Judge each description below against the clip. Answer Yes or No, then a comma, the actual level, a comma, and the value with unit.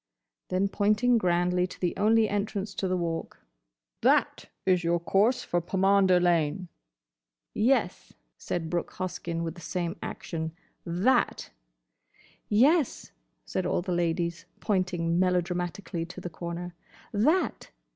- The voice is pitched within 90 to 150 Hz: No, medium, 180 Hz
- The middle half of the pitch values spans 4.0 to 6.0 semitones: No, average, 2.8 semitones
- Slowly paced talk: Yes, slow, 125 wpm